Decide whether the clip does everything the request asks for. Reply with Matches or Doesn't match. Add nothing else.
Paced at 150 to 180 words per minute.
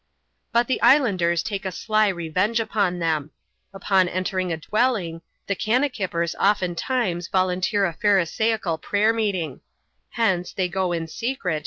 Doesn't match